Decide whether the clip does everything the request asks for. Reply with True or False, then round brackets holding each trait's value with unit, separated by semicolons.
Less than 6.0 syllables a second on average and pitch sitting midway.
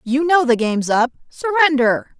False (5.8 syllables/s; 275 Hz)